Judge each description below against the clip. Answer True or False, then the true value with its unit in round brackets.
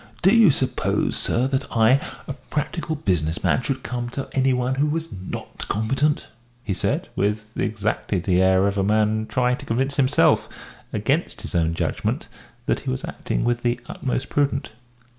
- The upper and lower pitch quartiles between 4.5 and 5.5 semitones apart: True (4.8 semitones)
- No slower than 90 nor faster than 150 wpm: False (175 wpm)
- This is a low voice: True (120 Hz)